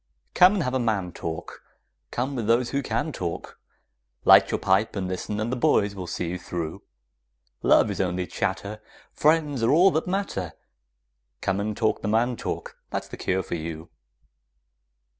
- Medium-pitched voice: No, low, 110 Hz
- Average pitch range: No, wide, 6.1 semitones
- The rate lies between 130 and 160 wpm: No, average, 175 wpm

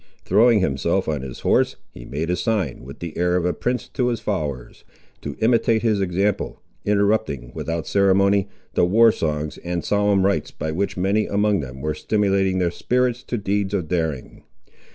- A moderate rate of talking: Yes, average, 175 wpm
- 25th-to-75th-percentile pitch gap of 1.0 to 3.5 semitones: No, average, 4.6 semitones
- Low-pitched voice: Yes, very low, 95 Hz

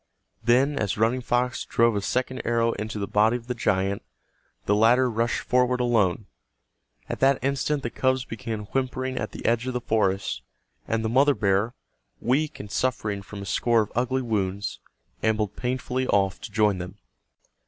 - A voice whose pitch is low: Yes, low, 115 Hz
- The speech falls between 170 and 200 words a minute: Yes, average, 175 wpm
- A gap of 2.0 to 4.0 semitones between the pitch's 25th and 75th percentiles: Yes, average, 3.5 semitones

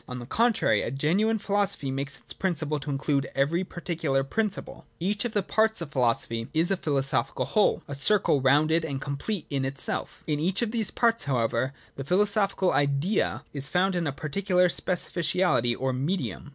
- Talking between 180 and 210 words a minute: Yes, average, 190 wpm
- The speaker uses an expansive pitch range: Yes, wide, 6.1 semitones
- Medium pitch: Yes, medium, 160 Hz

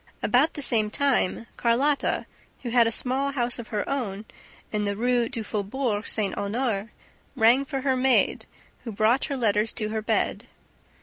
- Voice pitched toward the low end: No, high, 235 Hz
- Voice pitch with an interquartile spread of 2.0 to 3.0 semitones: No, average, 3.6 semitones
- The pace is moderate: Yes, average, 170 wpm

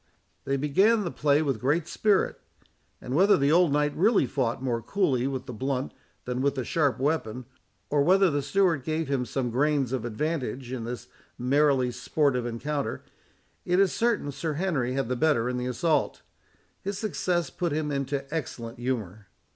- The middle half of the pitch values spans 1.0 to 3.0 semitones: No, average, 4.2 semitones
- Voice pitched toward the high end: No, medium, 140 Hz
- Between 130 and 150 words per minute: No, average, 175 wpm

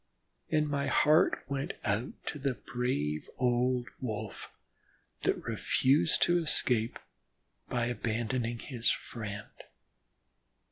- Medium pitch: No, low, 125 Hz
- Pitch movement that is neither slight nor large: Yes, average, 3.6 semitones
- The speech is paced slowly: Yes, slow, 100 wpm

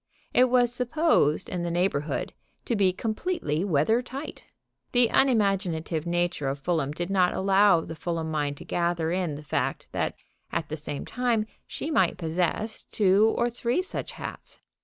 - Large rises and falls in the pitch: Yes, wide, 6.4 semitones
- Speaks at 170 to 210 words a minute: No, average, 160 wpm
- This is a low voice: No, medium, 185 Hz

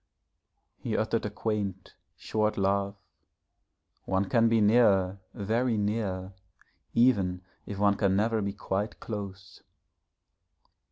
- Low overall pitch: Yes, low, 100 Hz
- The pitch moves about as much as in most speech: No, narrow, 2.2 semitones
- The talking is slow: Yes, slow, 110 wpm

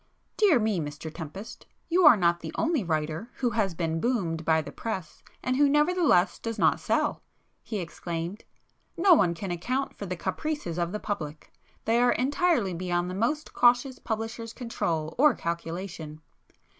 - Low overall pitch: No, high, 200 Hz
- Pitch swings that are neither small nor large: No, wide, 6.9 semitones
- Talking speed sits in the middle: Yes, average, 155 wpm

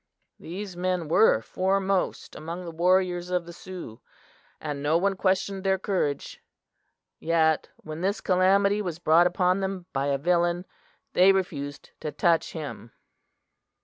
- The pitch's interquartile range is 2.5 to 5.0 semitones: Yes, average, 2.9 semitones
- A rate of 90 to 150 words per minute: Yes, average, 140 wpm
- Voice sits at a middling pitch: Yes, medium, 180 Hz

